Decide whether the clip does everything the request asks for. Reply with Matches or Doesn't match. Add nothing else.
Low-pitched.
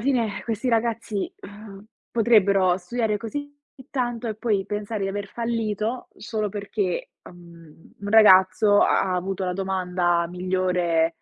Doesn't match